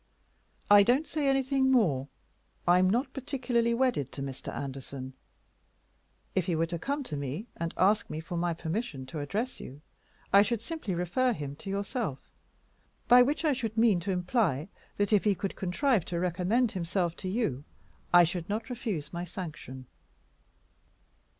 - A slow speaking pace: No, average, 165 wpm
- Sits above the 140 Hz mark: Yes, high, 190 Hz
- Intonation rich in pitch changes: Yes, wide, 6.5 semitones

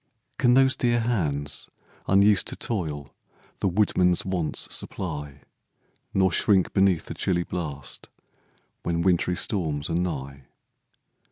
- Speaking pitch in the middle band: No, very low, 90 Hz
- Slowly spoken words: Yes, slow, 115 wpm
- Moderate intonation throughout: Yes, average, 4.8 semitones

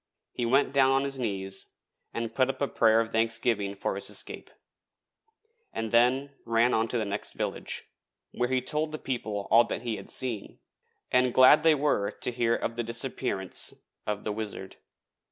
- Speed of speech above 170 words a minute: Yes, average, 180 wpm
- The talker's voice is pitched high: No, low, 115 Hz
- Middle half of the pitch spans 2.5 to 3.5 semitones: Yes, average, 3.0 semitones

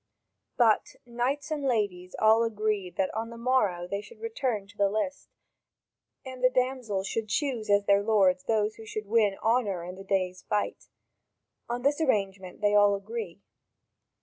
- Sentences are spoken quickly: No, average, 165 wpm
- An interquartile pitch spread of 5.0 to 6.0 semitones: No, average, 3.4 semitones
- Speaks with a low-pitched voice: No, high, 215 Hz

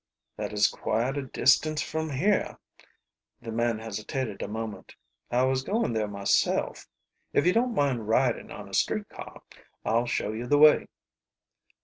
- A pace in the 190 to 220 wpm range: No, average, 155 wpm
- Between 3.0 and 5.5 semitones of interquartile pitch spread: Yes, average, 4.6 semitones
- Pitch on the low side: Yes, low, 120 Hz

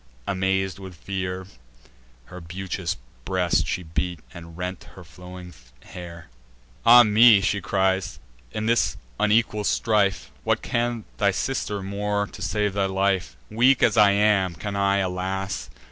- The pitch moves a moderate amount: No, narrow, 2.2 semitones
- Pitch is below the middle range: Yes, very low, 95 Hz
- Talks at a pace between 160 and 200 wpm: No, average, 140 wpm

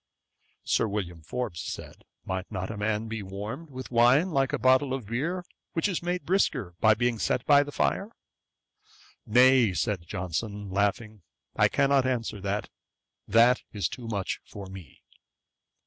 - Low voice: Yes, low, 115 Hz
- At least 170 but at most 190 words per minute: No, average, 155 wpm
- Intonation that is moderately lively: Yes, average, 4.7 semitones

